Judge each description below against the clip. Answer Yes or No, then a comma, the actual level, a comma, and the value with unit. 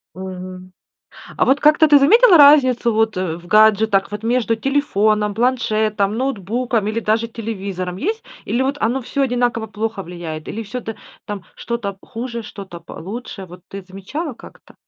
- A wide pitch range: No, average, 4.3 semitones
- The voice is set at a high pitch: Yes, high, 220 Hz